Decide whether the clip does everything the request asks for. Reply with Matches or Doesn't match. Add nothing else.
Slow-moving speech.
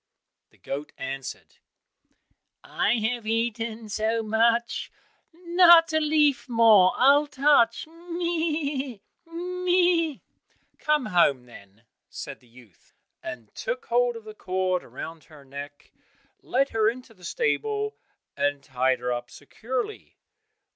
Matches